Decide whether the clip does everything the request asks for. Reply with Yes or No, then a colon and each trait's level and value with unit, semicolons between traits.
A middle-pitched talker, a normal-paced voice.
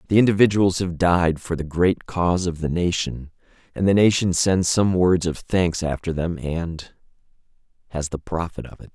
No: very low, 85 Hz; average, 175 wpm